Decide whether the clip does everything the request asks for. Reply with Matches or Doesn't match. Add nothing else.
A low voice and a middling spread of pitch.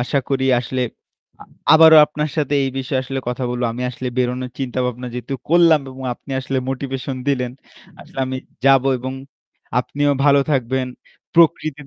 Doesn't match